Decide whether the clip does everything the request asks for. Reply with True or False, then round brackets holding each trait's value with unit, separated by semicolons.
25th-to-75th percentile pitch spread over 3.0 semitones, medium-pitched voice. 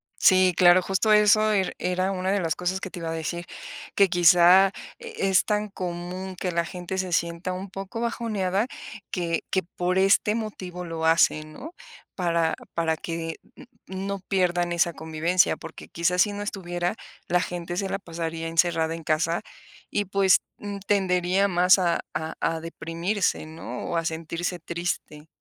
False (2.5 semitones; 180 Hz)